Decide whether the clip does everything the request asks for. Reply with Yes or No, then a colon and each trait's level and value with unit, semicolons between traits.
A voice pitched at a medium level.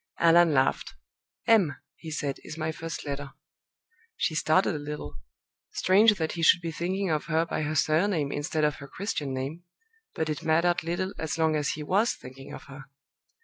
Yes: medium, 160 Hz